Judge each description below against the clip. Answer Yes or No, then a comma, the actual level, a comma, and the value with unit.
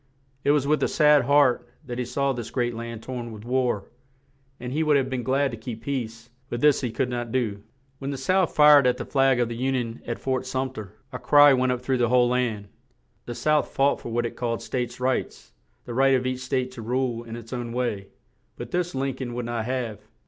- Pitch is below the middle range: Yes, low, 125 Hz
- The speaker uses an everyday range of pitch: No, narrow, 2.2 semitones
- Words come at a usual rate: No, fast, 235 wpm